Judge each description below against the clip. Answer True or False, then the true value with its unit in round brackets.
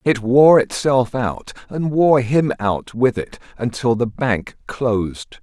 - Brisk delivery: False (155 wpm)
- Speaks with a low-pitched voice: True (120 Hz)